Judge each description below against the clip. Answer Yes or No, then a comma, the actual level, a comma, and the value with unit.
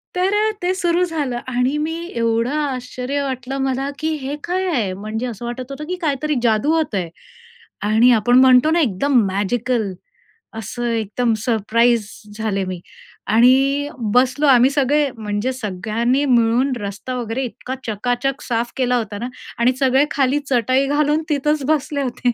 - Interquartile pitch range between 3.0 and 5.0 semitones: Yes, average, 3.7 semitones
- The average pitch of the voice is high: Yes, very high, 255 Hz